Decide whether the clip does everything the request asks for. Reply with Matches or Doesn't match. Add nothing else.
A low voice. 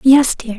Doesn't match